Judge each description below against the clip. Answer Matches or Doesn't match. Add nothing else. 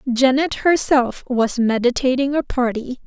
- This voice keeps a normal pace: Doesn't match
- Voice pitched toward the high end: Matches